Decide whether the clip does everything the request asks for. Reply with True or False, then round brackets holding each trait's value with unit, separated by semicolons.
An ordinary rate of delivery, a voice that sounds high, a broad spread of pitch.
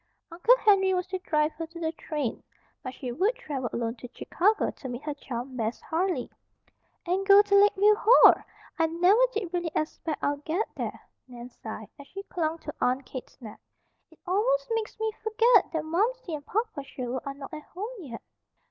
True (190 wpm; 330 Hz; 6.7 semitones)